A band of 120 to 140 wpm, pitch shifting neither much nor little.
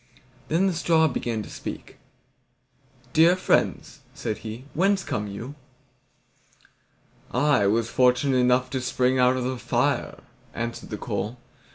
Yes: slow, 135 wpm; average, 4.2 semitones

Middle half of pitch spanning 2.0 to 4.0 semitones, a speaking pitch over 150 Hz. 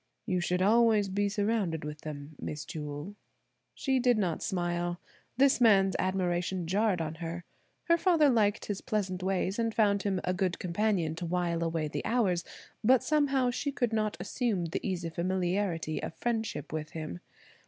No: average, 4.4 semitones; high, 190 Hz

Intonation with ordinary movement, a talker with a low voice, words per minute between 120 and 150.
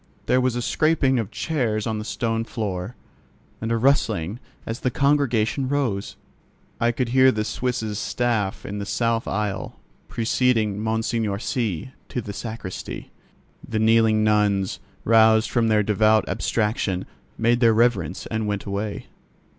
No: narrow, 2.3 semitones; low, 110 Hz; average, 145 wpm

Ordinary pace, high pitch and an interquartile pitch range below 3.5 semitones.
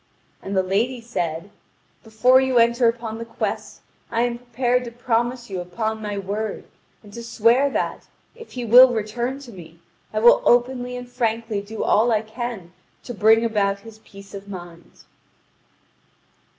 Yes: average, 165 wpm; high, 230 Hz; average, 3.0 semitones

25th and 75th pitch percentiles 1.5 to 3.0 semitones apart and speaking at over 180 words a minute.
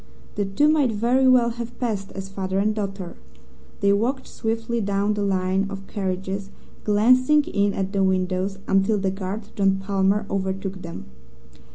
No: narrow, 2.5 semitones; average, 160 wpm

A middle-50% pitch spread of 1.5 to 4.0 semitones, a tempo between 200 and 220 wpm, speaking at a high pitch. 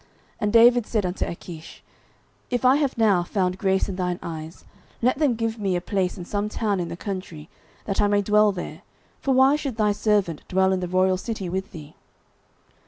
Yes: average, 3.5 semitones; fast, 205 wpm; high, 195 Hz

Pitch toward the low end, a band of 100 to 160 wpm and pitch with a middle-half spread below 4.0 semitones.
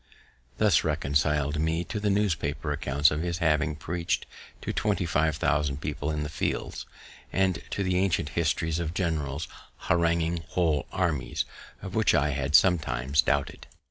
Yes: very low, 80 Hz; average, 150 wpm; average, 2.9 semitones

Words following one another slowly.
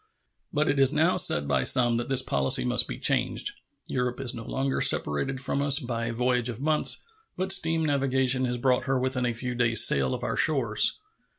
No: fast, 205 wpm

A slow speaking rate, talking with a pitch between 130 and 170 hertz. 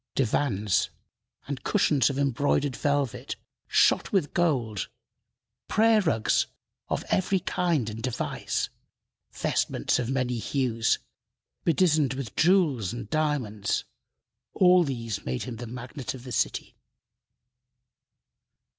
Yes: slow, 110 wpm; low, 135 Hz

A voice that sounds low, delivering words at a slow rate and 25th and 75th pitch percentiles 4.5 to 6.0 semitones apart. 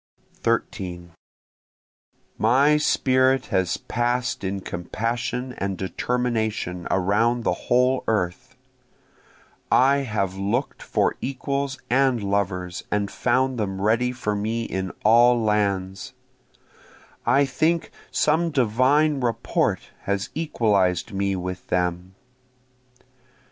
Yes: low, 115 Hz; slow, 100 wpm; average, 4.8 semitones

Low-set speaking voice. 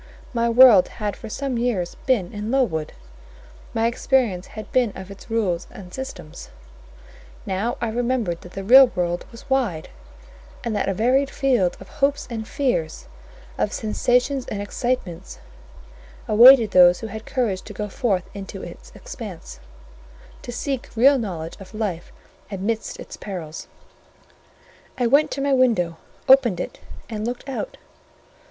No: high, 225 Hz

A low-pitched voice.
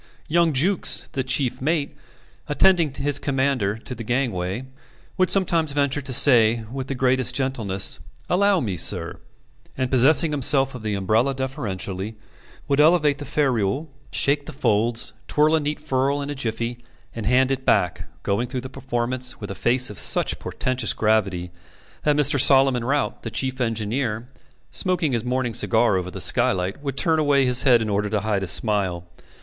Yes: low, 130 Hz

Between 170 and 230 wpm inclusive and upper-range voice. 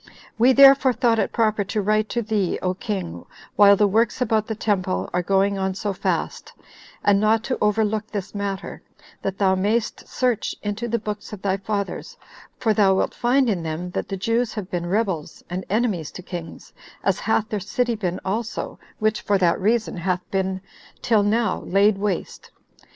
Yes: average, 185 wpm; high, 205 Hz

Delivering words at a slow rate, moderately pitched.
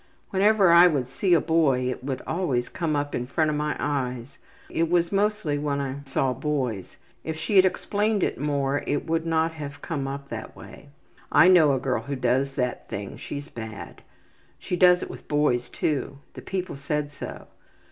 No: average, 190 wpm; medium, 145 Hz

